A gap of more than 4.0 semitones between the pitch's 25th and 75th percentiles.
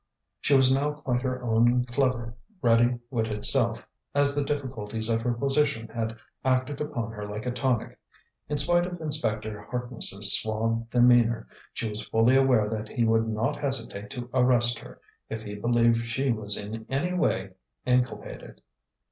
No: average, 2.9 semitones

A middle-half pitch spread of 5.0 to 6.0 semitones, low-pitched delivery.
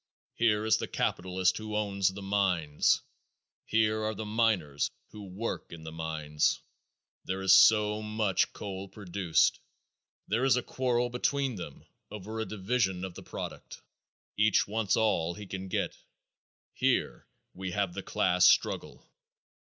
No: average, 3.0 semitones; low, 100 Hz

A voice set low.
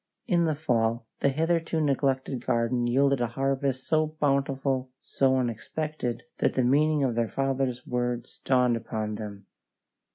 Yes: low, 130 Hz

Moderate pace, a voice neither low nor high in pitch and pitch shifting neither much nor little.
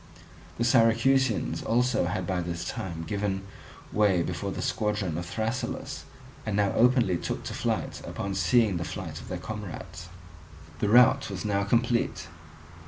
No: average, 150 wpm; low, 105 Hz; average, 4.1 semitones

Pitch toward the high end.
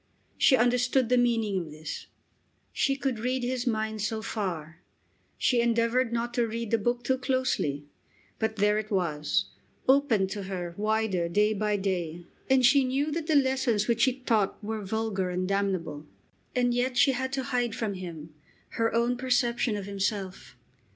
Yes: high, 225 Hz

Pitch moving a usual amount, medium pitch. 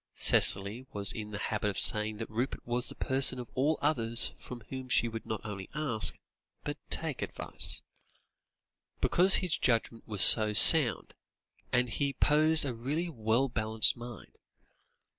No: average, 3.8 semitones; low, 120 Hz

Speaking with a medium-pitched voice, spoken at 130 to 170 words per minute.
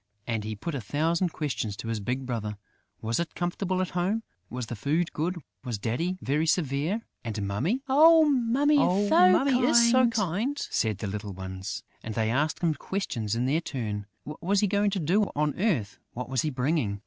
No: medium, 155 Hz; average, 190 wpm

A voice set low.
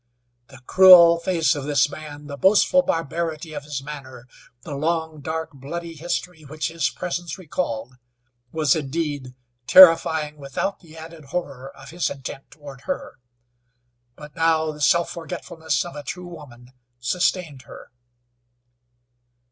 No: medium, 155 Hz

